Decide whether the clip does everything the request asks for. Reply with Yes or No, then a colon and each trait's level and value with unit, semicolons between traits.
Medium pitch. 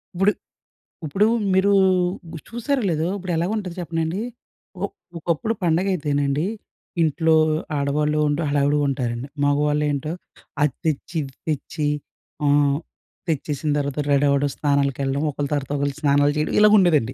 Yes: medium, 150 Hz